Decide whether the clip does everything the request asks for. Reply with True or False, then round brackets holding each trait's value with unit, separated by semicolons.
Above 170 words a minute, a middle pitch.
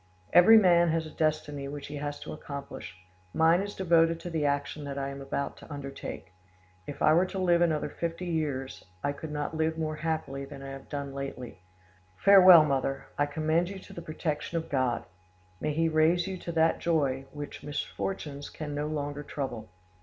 True (190 wpm; 150 Hz)